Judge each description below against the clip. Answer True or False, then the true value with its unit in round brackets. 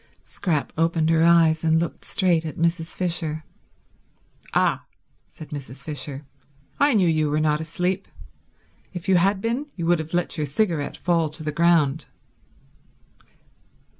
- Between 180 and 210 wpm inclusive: False (145 wpm)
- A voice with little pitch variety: True (2.2 semitones)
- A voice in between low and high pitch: True (165 Hz)